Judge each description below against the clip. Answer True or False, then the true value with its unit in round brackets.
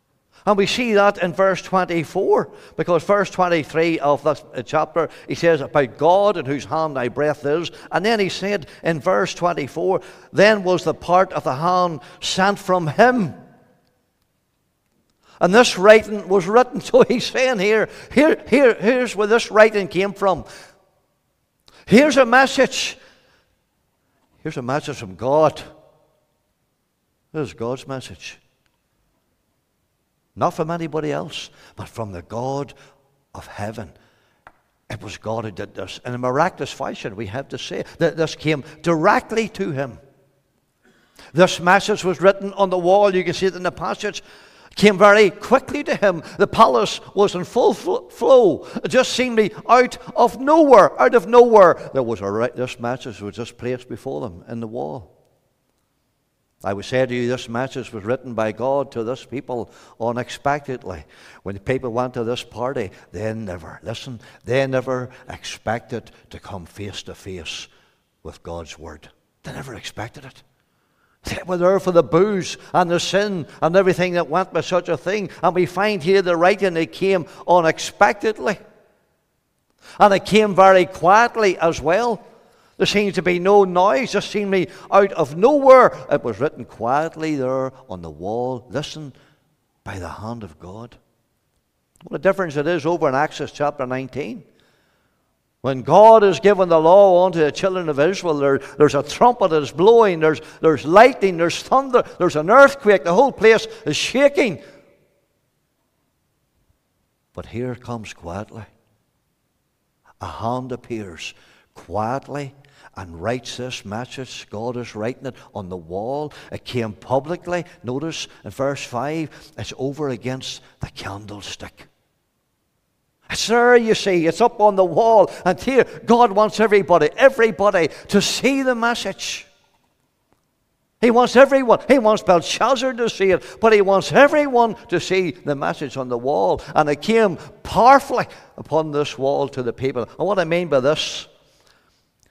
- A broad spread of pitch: True (7.7 semitones)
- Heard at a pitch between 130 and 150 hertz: False (160 Hz)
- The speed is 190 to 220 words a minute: False (160 wpm)